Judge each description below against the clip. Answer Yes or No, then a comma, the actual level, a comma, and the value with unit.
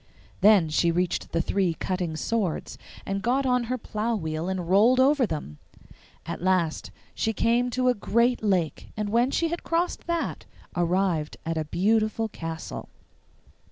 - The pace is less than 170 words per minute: Yes, average, 155 wpm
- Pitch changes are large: Yes, wide, 5.9 semitones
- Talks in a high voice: Yes, high, 200 Hz